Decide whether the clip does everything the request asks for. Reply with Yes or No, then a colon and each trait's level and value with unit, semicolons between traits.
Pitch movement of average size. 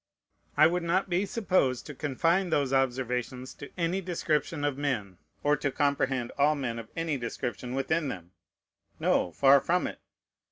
Yes: average, 4.5 semitones